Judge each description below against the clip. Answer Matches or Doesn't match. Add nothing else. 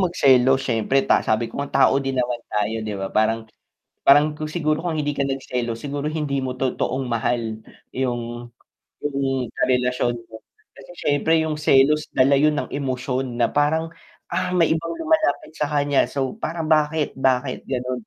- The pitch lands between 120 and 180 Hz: Matches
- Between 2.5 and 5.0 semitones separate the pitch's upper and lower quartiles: Matches